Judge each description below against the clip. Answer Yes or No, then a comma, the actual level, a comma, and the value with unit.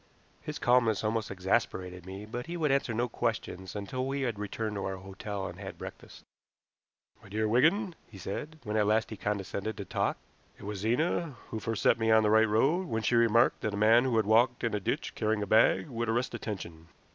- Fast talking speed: Yes, fast, 215 wpm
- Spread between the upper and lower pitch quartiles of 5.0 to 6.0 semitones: No, average, 3.0 semitones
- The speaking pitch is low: Yes, low, 110 Hz